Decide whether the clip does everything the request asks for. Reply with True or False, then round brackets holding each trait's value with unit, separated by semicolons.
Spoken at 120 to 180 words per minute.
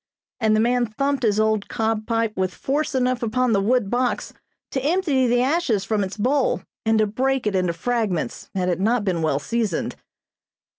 False (190 wpm)